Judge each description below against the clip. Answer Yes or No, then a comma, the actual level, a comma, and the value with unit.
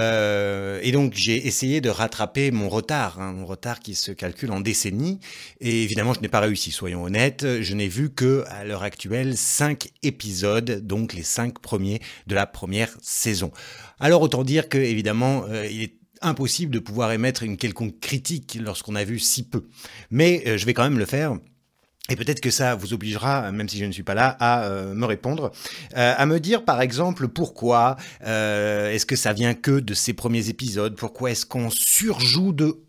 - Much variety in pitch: No, average, 4.2 semitones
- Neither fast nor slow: Yes, average, 190 wpm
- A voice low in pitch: Yes, low, 115 Hz